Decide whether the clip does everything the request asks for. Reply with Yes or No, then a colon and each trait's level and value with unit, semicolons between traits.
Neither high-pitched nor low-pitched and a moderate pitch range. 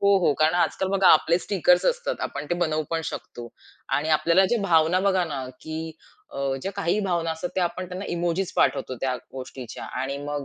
Yes: medium, 170 Hz; average, 3.2 semitones